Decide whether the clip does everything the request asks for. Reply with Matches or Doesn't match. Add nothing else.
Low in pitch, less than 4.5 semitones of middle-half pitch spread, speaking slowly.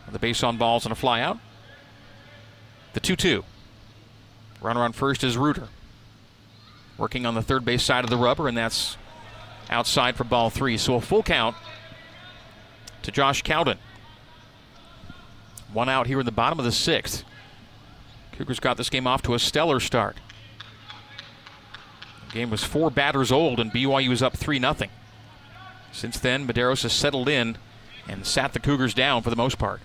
Doesn't match